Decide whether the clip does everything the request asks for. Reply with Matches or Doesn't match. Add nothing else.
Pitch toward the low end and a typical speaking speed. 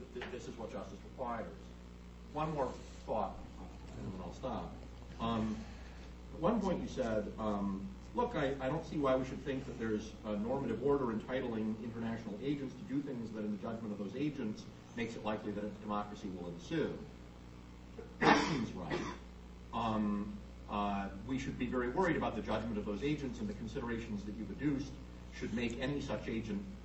Matches